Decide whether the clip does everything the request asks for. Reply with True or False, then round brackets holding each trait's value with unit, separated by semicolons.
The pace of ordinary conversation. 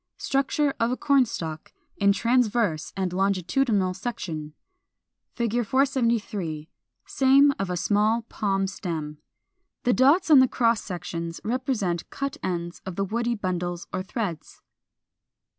False (125 wpm)